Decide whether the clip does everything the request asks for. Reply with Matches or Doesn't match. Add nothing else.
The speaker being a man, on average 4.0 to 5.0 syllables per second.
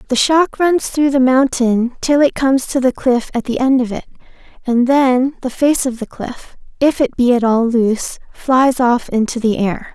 Doesn't match